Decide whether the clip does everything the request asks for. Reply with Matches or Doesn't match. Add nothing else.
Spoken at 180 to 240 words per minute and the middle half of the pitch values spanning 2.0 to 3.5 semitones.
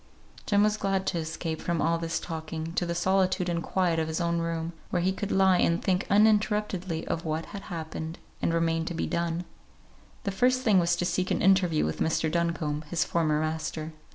Matches